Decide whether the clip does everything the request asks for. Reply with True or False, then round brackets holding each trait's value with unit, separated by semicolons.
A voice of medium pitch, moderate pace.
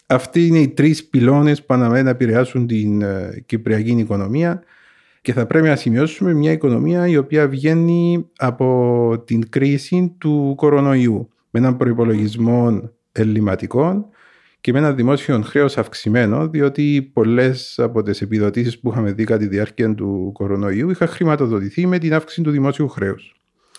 False (130 Hz; 145 wpm)